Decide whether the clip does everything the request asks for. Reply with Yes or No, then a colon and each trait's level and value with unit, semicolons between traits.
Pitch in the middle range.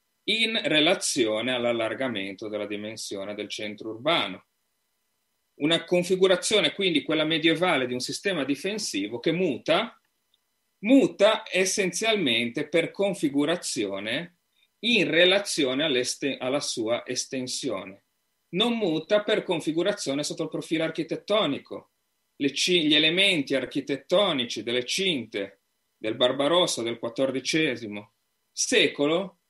Yes: medium, 160 Hz